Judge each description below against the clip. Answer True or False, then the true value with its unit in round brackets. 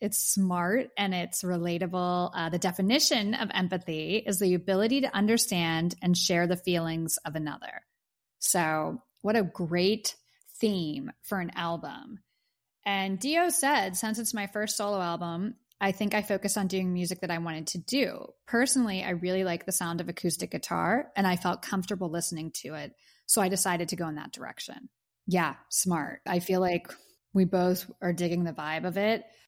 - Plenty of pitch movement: False (3.3 semitones)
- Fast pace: False (175 wpm)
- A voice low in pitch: False (185 Hz)